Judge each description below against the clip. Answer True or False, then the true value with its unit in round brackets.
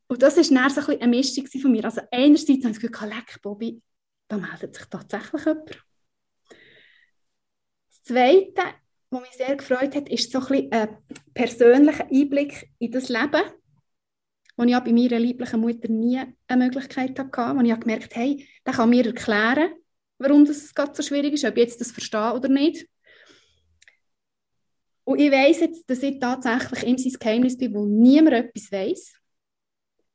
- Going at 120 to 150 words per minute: False (170 wpm)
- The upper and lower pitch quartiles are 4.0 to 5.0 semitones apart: False (3.5 semitones)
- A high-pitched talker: True (255 Hz)